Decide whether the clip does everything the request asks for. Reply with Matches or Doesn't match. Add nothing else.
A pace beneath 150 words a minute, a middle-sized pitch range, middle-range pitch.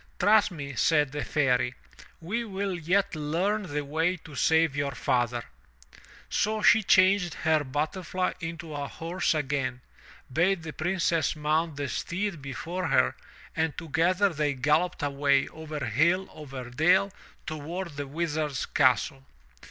Matches